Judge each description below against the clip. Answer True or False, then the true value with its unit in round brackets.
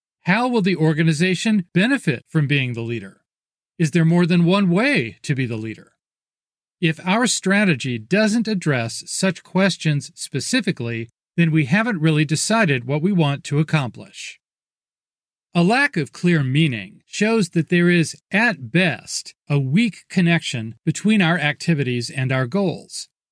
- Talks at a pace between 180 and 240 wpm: False (145 wpm)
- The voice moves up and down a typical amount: True (4.7 semitones)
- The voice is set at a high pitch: False (165 Hz)